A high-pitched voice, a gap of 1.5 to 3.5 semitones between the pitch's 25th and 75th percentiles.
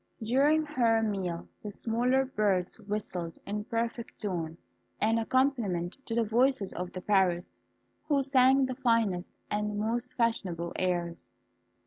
No: high, 215 Hz; average, 5.0 semitones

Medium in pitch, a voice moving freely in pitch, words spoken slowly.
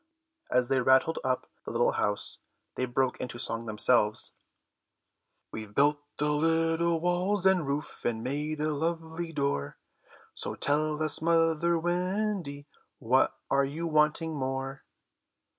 No: medium, 150 Hz; average, 3.8 semitones; slow, 130 wpm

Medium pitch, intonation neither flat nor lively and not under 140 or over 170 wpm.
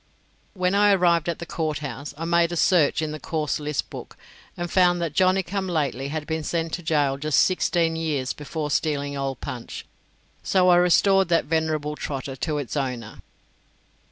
No: medium, 160 Hz; average, 3.2 semitones; average, 185 wpm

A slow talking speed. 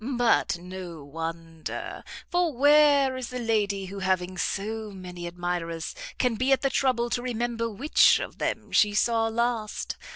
No: average, 155 wpm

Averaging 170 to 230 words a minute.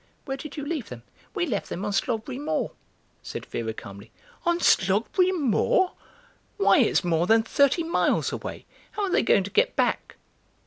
Yes: average, 175 wpm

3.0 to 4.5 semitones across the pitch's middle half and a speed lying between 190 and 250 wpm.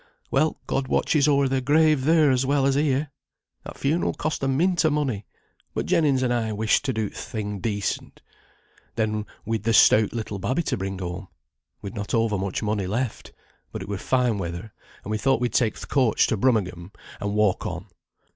No: average, 4.9 semitones; average, 195 wpm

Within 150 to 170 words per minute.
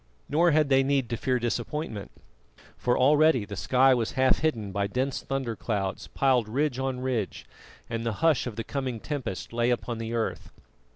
No: average, 180 wpm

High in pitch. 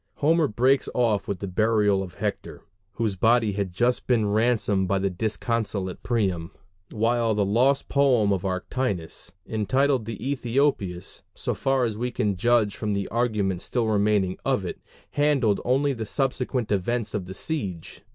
No: low, 110 Hz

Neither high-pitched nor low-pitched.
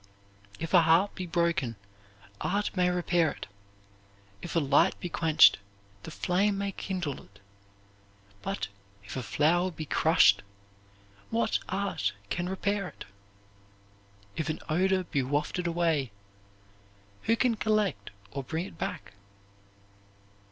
Yes: medium, 170 Hz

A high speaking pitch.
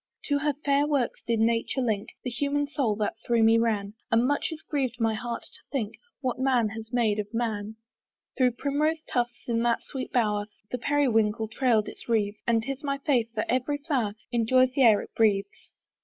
Yes: high, 240 Hz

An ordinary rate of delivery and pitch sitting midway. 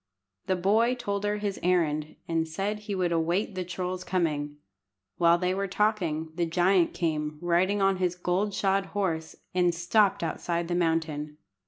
Yes: average, 165 wpm; medium, 180 Hz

